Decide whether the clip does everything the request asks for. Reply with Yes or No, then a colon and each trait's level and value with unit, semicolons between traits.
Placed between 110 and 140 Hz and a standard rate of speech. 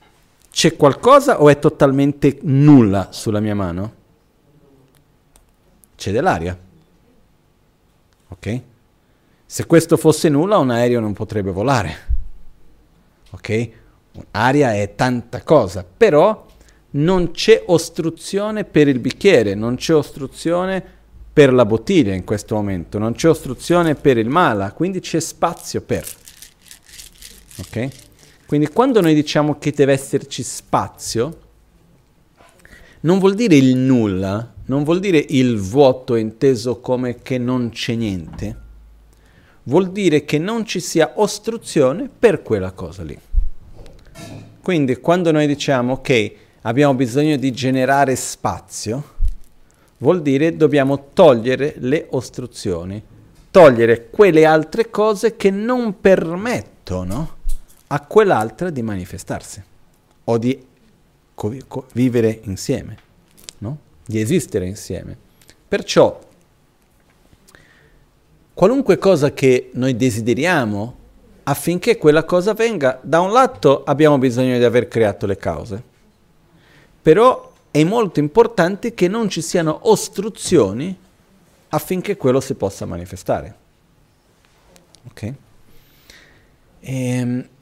No: low, 135 Hz; slow, 110 wpm